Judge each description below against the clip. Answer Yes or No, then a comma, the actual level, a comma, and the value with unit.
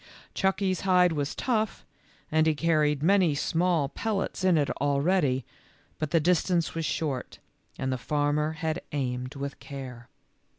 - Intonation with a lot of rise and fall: No, average, 4.2 semitones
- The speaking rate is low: No, average, 155 wpm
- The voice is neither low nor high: Yes, medium, 155 Hz